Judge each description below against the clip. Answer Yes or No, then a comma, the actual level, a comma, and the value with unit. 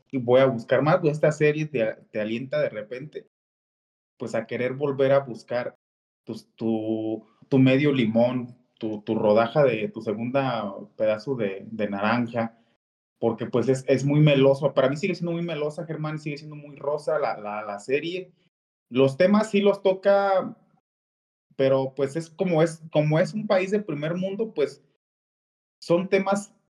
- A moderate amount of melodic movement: No, wide, 6.7 semitones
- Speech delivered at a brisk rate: No, average, 165 wpm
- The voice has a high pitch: No, medium, 140 Hz